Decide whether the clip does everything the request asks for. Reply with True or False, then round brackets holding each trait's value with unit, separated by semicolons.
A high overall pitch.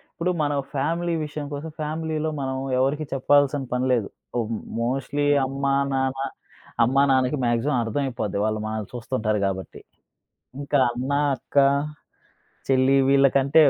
False (135 Hz)